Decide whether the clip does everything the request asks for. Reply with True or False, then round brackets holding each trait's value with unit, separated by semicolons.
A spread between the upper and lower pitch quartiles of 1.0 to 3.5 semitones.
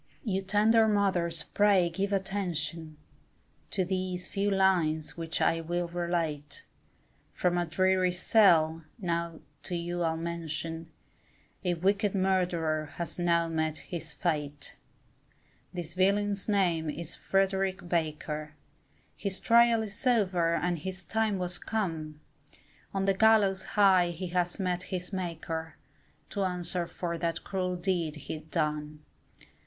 True (2.8 semitones)